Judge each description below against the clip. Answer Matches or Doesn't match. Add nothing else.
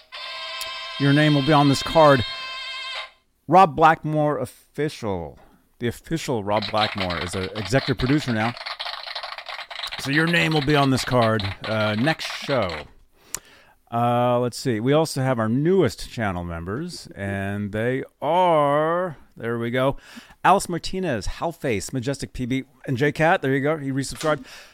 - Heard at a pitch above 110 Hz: Matches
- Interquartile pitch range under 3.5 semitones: Doesn't match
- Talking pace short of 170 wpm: Matches